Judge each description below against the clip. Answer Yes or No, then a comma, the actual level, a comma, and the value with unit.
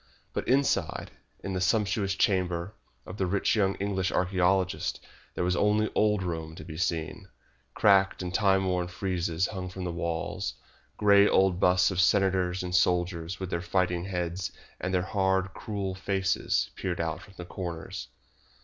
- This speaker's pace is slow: No, average, 160 wpm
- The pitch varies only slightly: Yes, narrow, 1.7 semitones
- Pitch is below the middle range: Yes, very low, 95 Hz